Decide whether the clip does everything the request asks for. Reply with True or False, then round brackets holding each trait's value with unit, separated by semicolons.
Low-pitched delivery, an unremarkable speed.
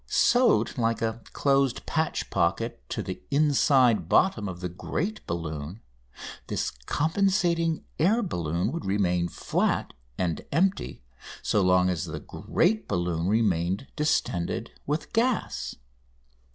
False (115 Hz; 125 wpm)